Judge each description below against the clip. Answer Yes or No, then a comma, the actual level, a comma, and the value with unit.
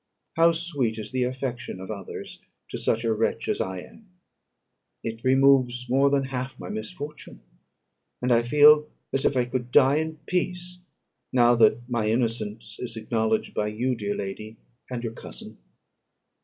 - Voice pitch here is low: Yes, low, 125 Hz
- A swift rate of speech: No, average, 160 wpm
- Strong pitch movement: No, average, 3.8 semitones